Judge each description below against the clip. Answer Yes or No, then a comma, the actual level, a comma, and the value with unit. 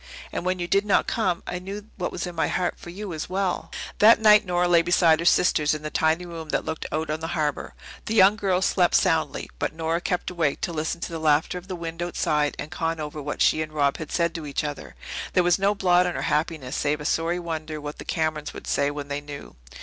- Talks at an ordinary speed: No, fast, 250 wpm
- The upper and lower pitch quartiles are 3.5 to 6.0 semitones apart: No, average, 2.8 semitones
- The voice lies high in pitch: No, medium, 165 Hz